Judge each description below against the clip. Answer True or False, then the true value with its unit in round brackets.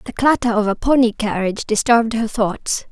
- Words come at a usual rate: True (185 wpm)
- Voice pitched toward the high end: True (225 Hz)